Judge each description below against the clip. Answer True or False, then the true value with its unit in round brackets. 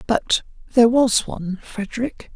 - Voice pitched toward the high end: True (230 Hz)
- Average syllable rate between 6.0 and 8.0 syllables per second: False (5.1 syllables/s)